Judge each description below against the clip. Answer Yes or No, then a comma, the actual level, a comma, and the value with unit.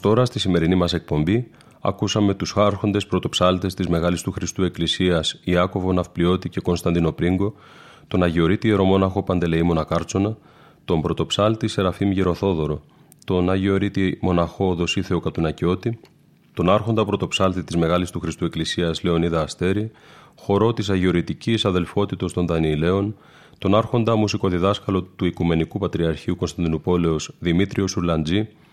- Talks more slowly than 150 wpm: Yes, average, 120 wpm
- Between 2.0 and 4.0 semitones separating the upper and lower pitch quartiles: Yes, average, 2.9 semitones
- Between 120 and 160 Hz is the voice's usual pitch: No, very low, 90 Hz